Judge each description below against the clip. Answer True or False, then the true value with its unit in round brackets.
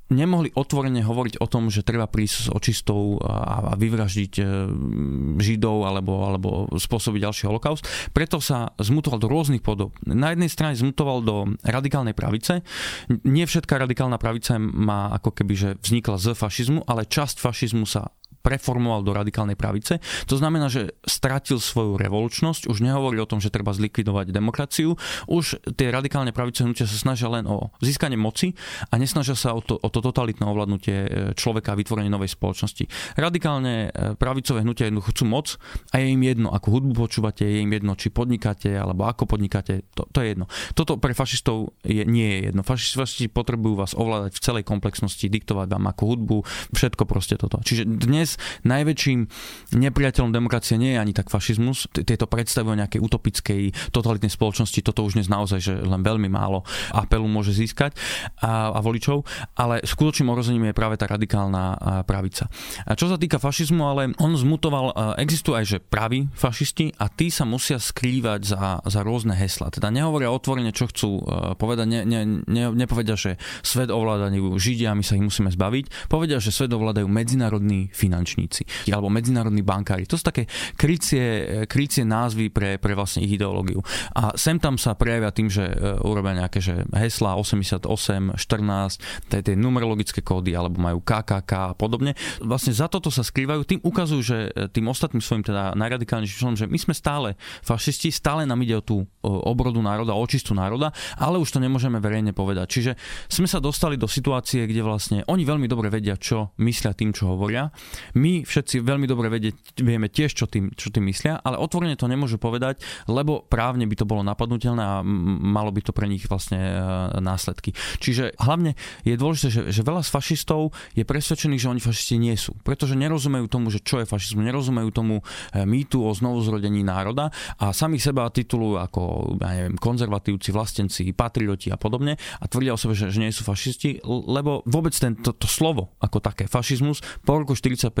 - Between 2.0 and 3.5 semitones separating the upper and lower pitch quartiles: False (4.2 semitones)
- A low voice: True (115 Hz)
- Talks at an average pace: False (175 wpm)